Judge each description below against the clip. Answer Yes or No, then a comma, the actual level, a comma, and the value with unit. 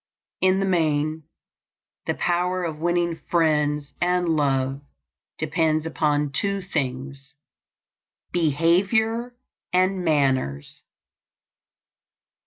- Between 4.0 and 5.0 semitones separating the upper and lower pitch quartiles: No, average, 3.5 semitones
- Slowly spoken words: Yes, slow, 80 wpm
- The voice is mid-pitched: Yes, medium, 160 Hz